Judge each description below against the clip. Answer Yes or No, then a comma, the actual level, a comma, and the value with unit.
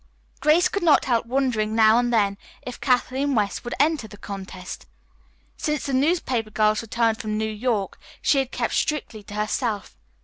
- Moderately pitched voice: No, high, 230 Hz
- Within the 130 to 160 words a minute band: No, average, 170 wpm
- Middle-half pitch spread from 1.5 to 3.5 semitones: No, average, 3.9 semitones